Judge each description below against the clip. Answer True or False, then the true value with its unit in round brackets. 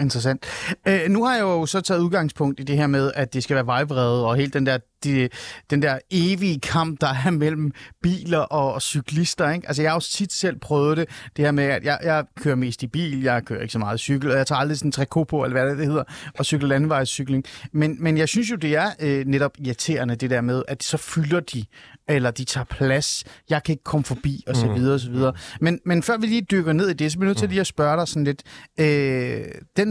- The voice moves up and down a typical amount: True (3.3 semitones)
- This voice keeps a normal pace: False (255 wpm)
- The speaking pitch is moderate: True (145 Hz)